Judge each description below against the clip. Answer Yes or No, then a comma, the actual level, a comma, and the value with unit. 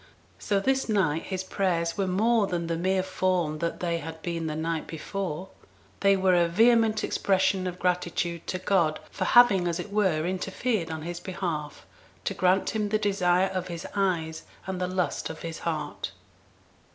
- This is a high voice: No, medium, 180 Hz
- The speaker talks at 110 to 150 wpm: No, average, 175 wpm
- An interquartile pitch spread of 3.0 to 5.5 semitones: No, narrow, 2.6 semitones